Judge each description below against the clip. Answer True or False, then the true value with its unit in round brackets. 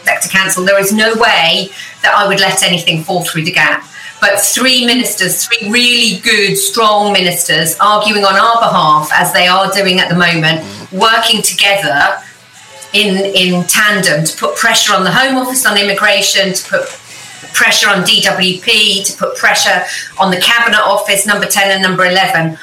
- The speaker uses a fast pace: False (170 wpm)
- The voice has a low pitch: False (195 Hz)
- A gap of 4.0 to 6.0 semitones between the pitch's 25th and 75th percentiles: False (2.7 semitones)